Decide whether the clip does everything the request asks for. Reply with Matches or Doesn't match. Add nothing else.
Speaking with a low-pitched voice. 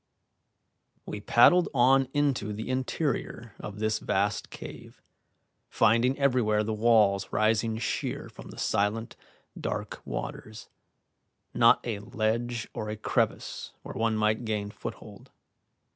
Matches